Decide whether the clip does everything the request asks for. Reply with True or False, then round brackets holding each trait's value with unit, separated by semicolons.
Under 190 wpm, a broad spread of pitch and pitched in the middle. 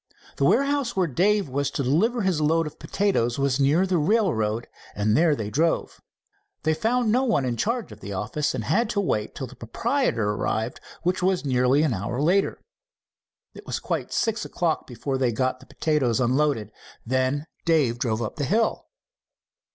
True (180 wpm; 7.6 semitones; 150 Hz)